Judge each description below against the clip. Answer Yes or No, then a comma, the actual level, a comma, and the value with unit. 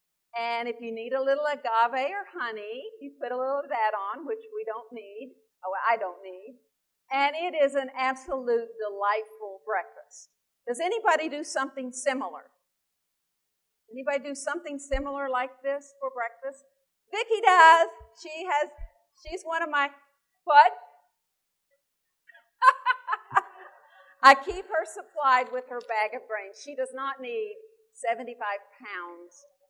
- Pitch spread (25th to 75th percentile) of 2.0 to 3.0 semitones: No, average, 4.9 semitones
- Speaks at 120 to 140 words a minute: Yes, slow, 135 wpm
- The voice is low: No, very high, 270 Hz